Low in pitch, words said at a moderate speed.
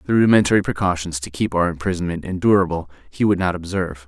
Yes: very low, 90 Hz; average, 175 wpm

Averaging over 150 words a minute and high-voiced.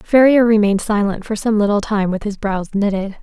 Yes: fast, 205 wpm; high, 210 Hz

